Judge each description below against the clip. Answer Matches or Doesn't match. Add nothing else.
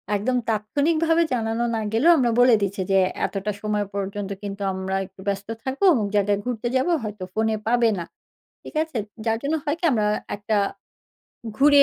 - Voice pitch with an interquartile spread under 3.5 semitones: Doesn't match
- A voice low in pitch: Doesn't match